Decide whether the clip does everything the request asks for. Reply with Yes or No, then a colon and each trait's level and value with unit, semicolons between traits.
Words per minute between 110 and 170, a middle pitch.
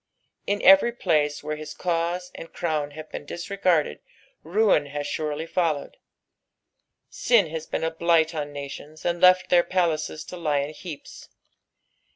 Yes: average, 150 wpm; medium, 160 Hz